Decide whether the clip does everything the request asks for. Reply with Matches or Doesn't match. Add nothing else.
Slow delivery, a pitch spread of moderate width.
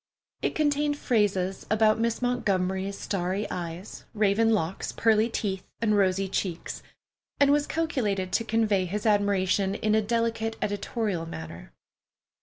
Matches